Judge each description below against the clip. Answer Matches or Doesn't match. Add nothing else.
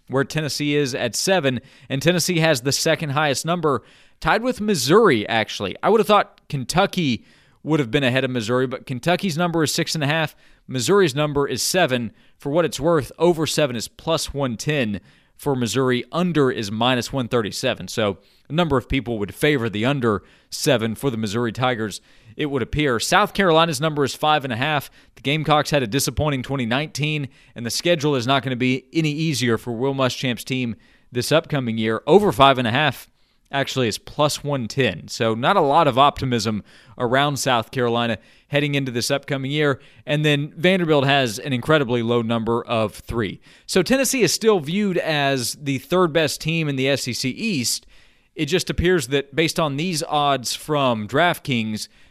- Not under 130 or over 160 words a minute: Doesn't match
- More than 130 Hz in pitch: Matches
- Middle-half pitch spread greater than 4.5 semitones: Doesn't match